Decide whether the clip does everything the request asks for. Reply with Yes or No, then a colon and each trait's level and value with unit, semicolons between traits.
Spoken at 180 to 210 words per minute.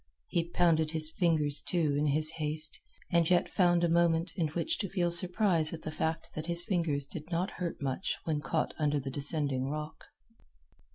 Yes: average, 185 wpm